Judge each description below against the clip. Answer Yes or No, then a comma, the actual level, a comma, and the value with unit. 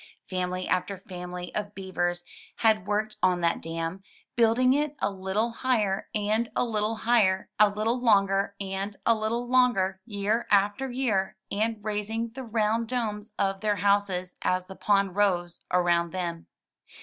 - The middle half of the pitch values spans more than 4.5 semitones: No, average, 3.0 semitones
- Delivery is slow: No, average, 150 wpm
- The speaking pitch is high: Yes, high, 205 Hz